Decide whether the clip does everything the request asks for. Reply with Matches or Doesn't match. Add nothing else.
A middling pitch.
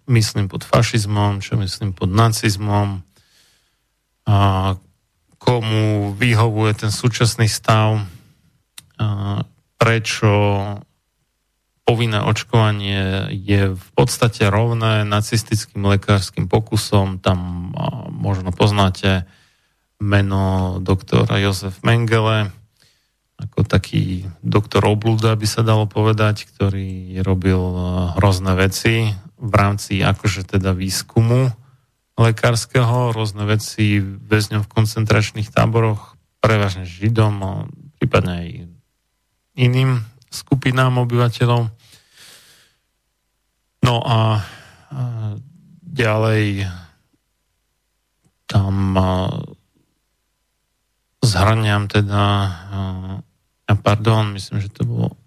Doesn't match